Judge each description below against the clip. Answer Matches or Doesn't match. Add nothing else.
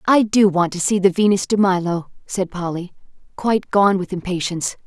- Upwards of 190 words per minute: Doesn't match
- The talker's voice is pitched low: Doesn't match